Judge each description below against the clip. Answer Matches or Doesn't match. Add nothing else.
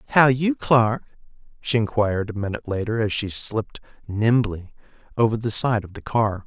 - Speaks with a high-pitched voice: Doesn't match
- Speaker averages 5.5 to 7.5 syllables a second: Doesn't match